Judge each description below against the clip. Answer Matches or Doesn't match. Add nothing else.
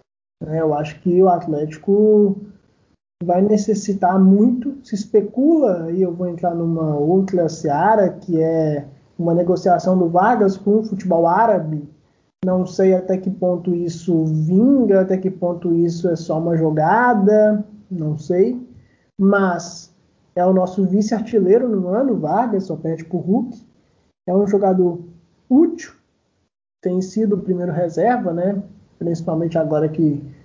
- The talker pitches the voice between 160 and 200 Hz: Matches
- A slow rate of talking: Doesn't match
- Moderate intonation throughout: Matches